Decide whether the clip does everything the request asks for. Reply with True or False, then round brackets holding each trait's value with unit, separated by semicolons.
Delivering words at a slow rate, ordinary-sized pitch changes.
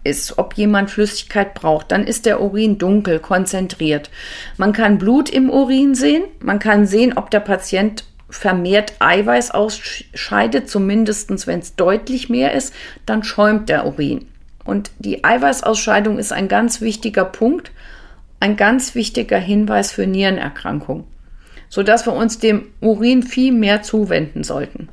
False (145 wpm; 3.0 semitones)